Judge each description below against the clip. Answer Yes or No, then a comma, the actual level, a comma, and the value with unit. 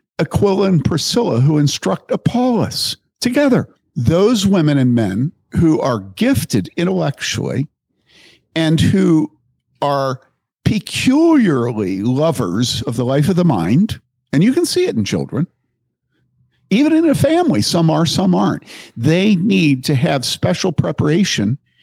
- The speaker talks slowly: Yes, slow, 130 wpm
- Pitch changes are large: Yes, wide, 6.4 semitones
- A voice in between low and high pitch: Yes, medium, 160 Hz